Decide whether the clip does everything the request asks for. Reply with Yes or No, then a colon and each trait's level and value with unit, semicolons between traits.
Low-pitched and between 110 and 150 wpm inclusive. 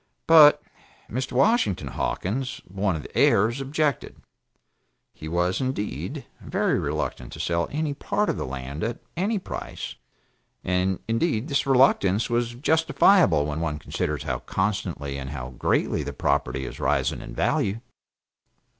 Yes: low, 105 Hz; average, 140 wpm